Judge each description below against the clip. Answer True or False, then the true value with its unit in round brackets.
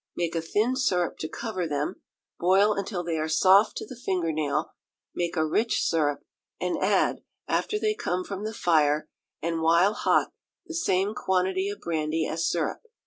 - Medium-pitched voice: True (175 Hz)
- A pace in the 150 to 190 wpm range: True (175 wpm)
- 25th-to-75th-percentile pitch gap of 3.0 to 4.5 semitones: True (3.9 semitones)